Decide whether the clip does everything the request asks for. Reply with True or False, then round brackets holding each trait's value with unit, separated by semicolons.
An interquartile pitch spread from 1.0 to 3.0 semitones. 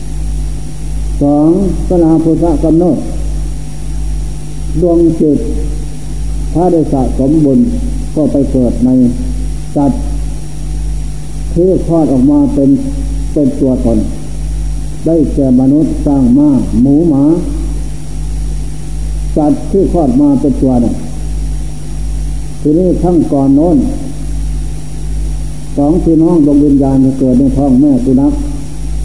True (2.6 semitones)